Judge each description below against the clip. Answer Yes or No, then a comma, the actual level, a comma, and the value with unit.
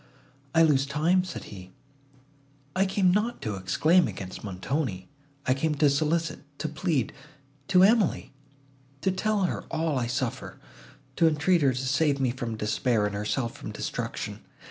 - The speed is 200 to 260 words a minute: No, average, 150 wpm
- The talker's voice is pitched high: No, medium, 145 Hz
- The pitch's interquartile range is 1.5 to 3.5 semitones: No, wide, 5.6 semitones